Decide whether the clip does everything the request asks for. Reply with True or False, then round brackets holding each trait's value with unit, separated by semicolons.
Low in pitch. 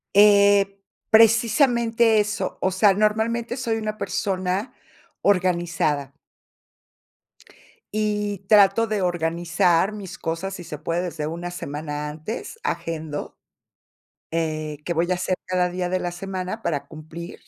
False (185 Hz)